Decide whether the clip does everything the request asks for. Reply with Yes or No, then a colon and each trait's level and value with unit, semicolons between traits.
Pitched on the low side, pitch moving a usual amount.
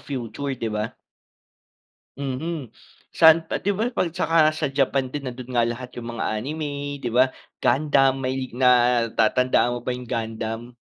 Yes: low, 130 Hz; average, 3.1 semitones